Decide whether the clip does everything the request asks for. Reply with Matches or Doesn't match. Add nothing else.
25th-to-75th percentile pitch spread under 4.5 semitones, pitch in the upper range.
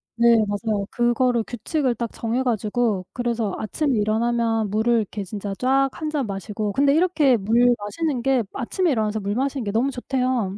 Matches